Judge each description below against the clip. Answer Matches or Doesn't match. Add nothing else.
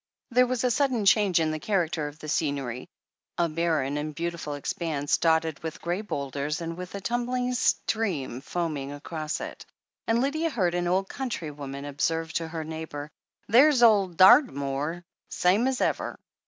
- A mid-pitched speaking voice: Matches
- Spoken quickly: Doesn't match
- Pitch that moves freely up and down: Matches